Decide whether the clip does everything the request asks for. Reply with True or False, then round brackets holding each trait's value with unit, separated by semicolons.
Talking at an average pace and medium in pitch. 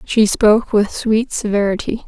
False (145 wpm; 215 Hz)